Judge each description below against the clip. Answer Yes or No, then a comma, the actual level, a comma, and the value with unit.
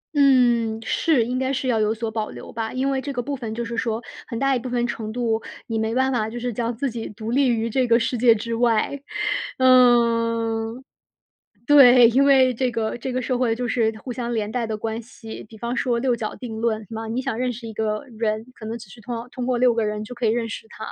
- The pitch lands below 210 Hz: No, high, 235 Hz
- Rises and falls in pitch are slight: Yes, narrow, 2.1 semitones